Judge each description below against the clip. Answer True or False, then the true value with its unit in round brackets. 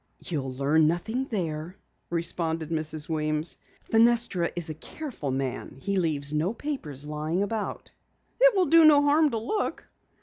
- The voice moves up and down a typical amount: False (7.4 semitones)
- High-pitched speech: False (170 Hz)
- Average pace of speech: True (145 wpm)